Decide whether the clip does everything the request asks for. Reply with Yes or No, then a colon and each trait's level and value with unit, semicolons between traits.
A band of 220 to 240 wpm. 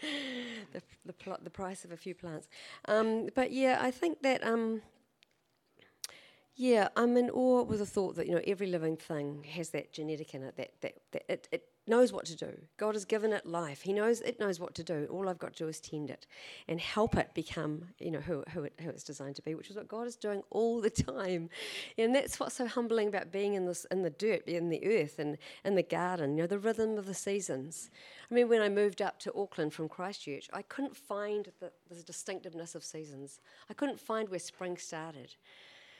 Yes: fast, 225 wpm